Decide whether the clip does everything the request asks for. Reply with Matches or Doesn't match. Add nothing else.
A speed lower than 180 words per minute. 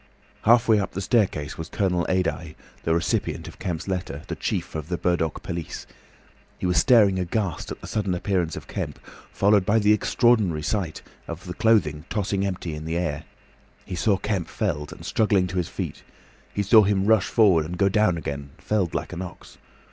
Doesn't match